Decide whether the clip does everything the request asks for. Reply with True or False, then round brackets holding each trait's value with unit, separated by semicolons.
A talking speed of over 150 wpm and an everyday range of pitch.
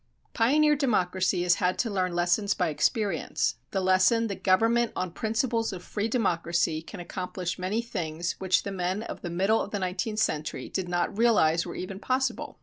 True (180 wpm; 4.0 semitones)